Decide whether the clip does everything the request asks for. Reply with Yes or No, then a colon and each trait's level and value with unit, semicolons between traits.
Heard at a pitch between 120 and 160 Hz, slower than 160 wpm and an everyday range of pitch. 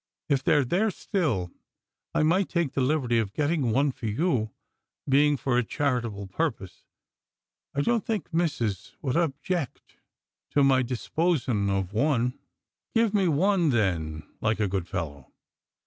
No: low, 135 Hz; average, 150 wpm; wide, 7.0 semitones